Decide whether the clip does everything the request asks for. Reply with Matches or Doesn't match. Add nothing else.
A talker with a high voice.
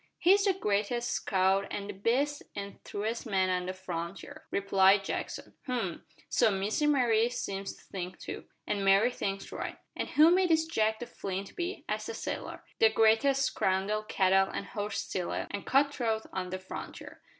Matches